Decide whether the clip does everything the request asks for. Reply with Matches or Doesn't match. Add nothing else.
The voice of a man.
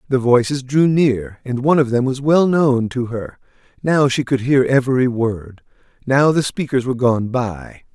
Matches